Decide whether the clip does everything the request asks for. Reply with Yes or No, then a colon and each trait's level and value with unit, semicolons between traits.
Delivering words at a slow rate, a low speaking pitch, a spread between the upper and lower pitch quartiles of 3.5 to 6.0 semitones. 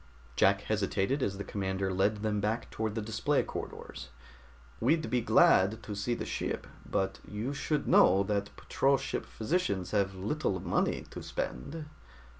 No: average, 155 wpm; low, 105 Hz; average, 3.8 semitones